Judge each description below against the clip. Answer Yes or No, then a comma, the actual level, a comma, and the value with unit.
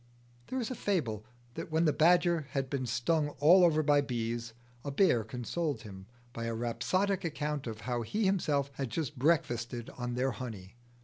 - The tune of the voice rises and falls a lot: Yes, wide, 5.7 semitones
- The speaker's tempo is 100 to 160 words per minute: No, average, 180 wpm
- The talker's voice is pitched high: No, medium, 140 Hz